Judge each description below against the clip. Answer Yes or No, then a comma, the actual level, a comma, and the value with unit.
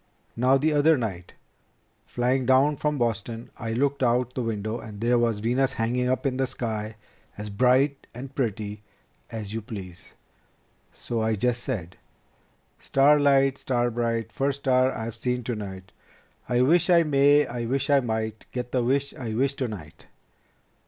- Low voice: Yes, low, 125 Hz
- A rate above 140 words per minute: Yes, average, 160 wpm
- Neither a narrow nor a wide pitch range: Yes, average, 3.4 semitones